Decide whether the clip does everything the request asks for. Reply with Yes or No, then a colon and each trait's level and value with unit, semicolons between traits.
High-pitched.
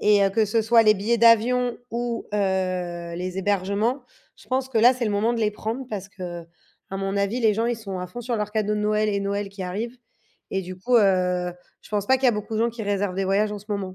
Yes: high, 210 Hz